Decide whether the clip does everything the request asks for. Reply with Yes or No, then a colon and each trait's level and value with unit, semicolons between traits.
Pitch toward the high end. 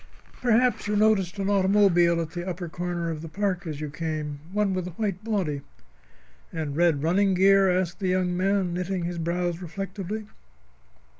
No: medium, 180 Hz